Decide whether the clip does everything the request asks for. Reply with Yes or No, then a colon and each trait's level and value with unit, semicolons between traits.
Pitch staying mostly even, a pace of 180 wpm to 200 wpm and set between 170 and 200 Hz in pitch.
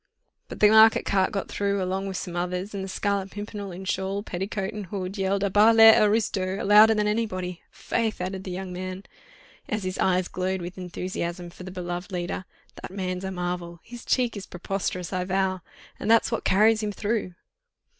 Yes: narrow, 2.2 semitones; average, 190 wpm; high, 190 Hz